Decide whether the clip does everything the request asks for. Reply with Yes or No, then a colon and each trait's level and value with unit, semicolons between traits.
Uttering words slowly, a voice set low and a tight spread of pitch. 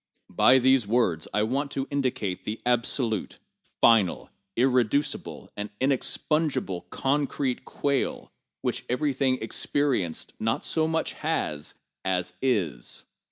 No: slow, 110 wpm; low, 125 Hz; average, 4.9 semitones